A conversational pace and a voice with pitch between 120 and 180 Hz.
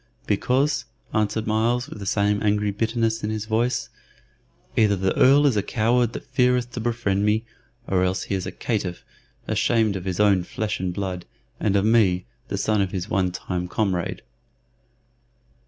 No: average, 170 wpm; low, 105 Hz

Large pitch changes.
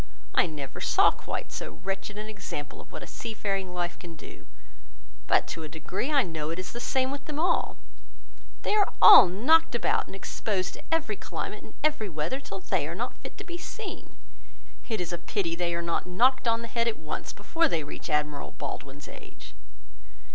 Yes: wide, 6.6 semitones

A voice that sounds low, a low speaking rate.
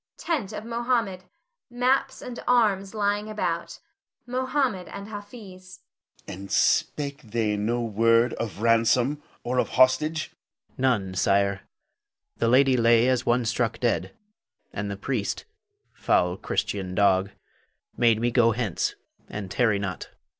Yes: low, 125 Hz; slow, 130 wpm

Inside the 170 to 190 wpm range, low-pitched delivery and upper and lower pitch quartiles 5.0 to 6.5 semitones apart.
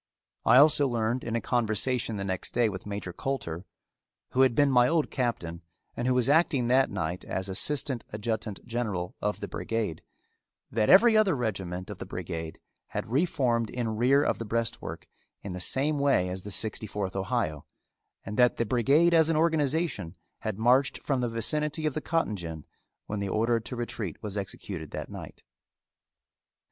Yes: average, 175 wpm; low, 115 Hz; average, 5.3 semitones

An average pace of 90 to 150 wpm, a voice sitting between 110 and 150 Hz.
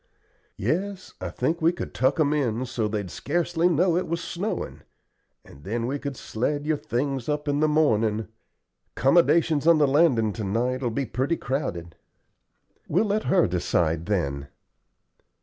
No: average, 160 wpm; medium, 140 Hz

